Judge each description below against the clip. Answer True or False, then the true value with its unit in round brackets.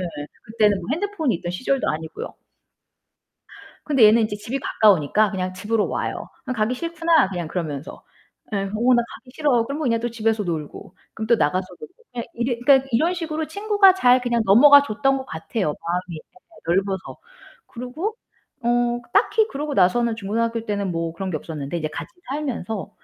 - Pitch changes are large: True (6.4 semitones)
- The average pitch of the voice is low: False (230 Hz)